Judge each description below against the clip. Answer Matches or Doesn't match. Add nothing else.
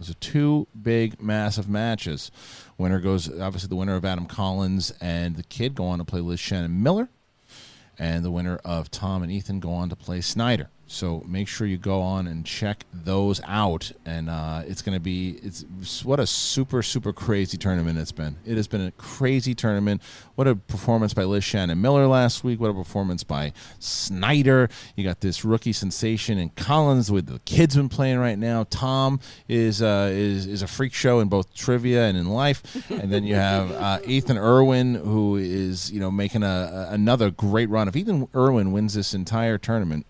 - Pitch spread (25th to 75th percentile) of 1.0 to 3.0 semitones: Doesn't match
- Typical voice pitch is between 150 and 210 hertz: Doesn't match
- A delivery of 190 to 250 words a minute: Matches